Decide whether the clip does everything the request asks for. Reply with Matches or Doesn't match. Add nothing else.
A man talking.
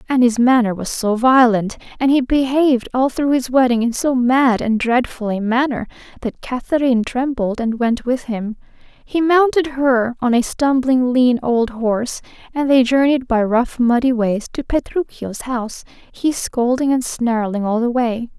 Doesn't match